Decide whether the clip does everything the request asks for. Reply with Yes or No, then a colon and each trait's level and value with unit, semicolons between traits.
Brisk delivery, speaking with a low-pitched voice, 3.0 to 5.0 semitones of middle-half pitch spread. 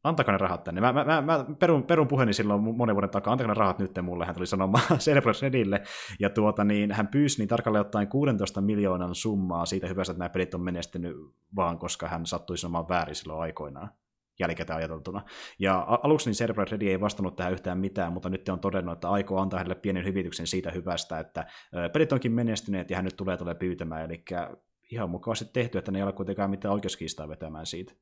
Yes: fast, 210 wpm; very low, 95 Hz; average, 3.5 semitones